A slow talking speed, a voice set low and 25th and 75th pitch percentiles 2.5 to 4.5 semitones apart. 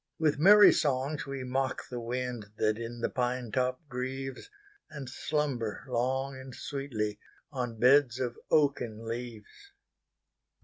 Yes: slow, 115 wpm; low, 130 Hz; average, 2.9 semitones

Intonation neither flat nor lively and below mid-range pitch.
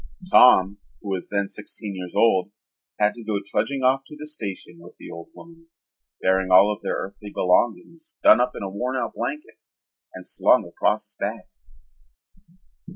Yes: average, 4.9 semitones; low, 105 Hz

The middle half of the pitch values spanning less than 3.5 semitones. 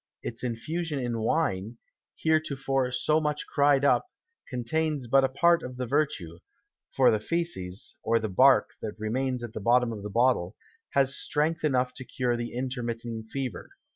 No: average, 3.8 semitones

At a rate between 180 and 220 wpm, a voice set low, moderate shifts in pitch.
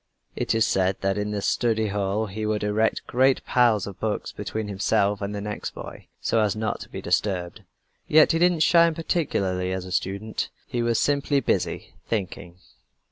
Yes: average, 190 wpm; low, 105 Hz; average, 3.2 semitones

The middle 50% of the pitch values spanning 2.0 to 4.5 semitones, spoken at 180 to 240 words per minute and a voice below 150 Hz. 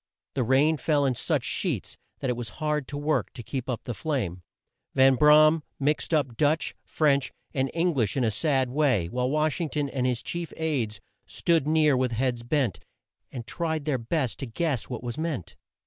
Yes: average, 3.8 semitones; average, 195 wpm; medium, 140 Hz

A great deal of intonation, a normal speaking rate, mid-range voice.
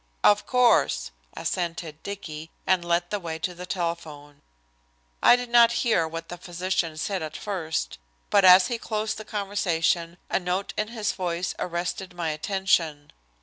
No: average, 3.4 semitones; average, 155 wpm; medium, 180 Hz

